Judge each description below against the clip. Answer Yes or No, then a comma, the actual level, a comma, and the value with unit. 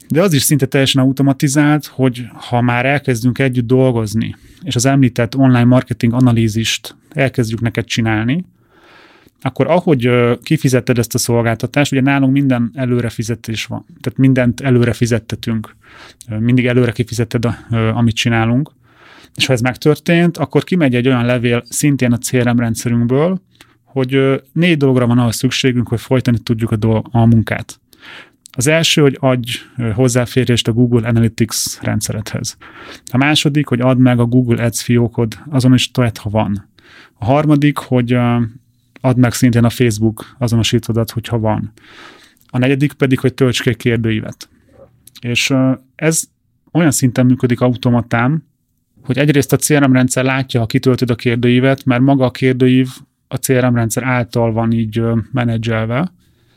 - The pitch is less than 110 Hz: No, low, 125 Hz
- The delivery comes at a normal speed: Yes, average, 145 wpm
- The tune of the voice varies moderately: No, narrow, 2.2 semitones